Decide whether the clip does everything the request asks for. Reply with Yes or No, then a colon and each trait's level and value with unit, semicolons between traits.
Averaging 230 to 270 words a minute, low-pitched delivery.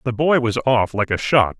Yes: fast, 265 wpm; low, 120 Hz